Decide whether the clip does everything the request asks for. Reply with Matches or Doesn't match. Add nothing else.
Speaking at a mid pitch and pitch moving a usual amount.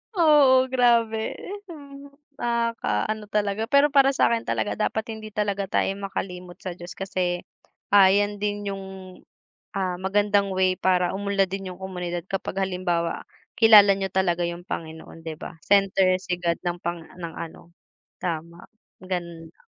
Doesn't match